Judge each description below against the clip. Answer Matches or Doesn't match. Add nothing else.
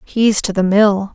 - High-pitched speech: Matches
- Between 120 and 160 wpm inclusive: Doesn't match